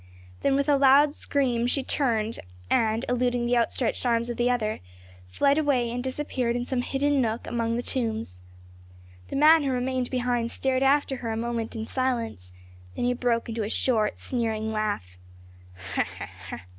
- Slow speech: No, average, 165 wpm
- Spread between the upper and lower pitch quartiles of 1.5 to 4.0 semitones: Yes, narrow, 2.5 semitones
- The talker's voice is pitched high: Yes, high, 245 Hz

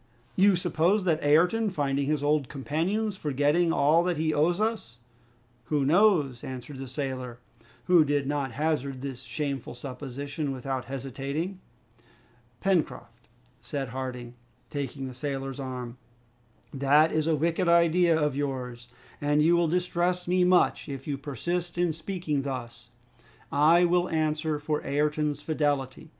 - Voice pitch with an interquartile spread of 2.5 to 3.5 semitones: No, average, 3.9 semitones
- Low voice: No, medium, 145 Hz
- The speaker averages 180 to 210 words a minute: No, average, 140 wpm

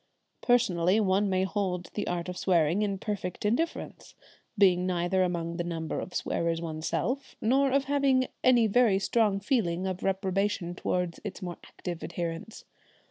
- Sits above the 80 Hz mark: Yes, high, 190 Hz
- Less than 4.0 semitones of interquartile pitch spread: Yes, average, 3.5 semitones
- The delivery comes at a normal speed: Yes, average, 145 wpm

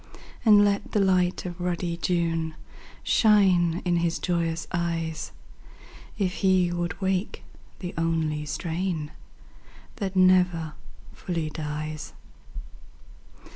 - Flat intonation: Yes, narrow, 2.2 semitones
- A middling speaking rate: No, slow, 100 wpm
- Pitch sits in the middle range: Yes, medium, 175 Hz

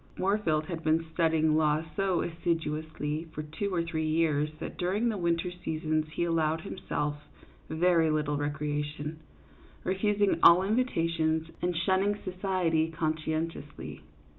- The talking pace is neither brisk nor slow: No, slow, 125 wpm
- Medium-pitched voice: Yes, medium, 160 Hz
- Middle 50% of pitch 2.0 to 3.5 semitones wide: Yes, narrow, 2.6 semitones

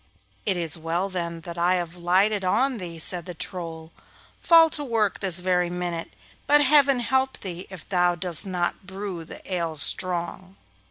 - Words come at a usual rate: Yes, average, 170 wpm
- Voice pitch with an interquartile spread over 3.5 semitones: No, average, 2.9 semitones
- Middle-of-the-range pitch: Yes, medium, 180 Hz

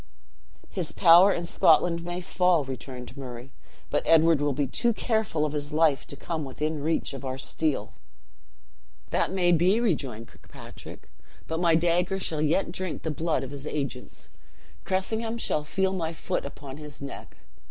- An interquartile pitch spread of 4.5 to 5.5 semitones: No, average, 4.0 semitones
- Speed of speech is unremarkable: Yes, average, 165 wpm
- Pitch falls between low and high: Yes, medium, 160 Hz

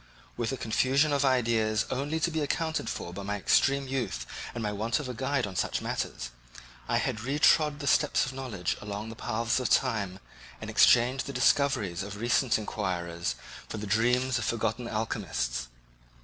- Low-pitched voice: Yes, low, 115 Hz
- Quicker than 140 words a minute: Yes, average, 175 wpm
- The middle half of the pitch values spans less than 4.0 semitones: No, average, 4.5 semitones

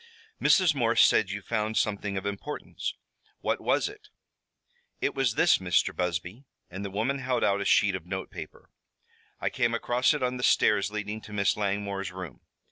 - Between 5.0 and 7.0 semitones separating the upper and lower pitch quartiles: No, average, 3.8 semitones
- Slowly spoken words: No, average, 180 wpm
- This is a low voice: Yes, low, 105 Hz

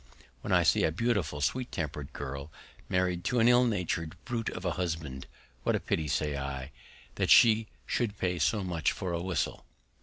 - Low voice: Yes, very low, 90 Hz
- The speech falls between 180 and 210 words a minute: Yes, average, 185 wpm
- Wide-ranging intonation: Yes, wide, 5.9 semitones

